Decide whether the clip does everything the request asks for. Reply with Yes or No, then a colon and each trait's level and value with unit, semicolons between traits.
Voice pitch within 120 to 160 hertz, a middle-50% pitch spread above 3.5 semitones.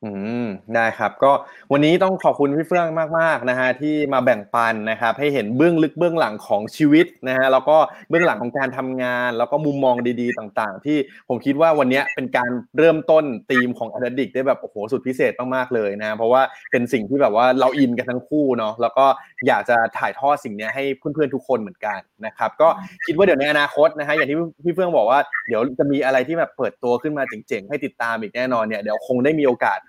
Yes: low, 135 Hz; average, 4.2 semitones